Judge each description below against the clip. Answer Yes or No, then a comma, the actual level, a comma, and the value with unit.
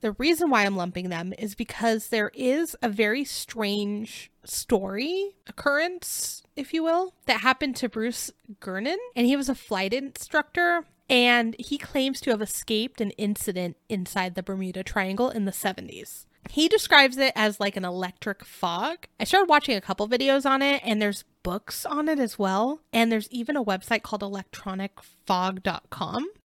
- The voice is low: No, high, 235 Hz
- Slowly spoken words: No, average, 170 wpm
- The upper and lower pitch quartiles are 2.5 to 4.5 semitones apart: No, wide, 5.6 semitones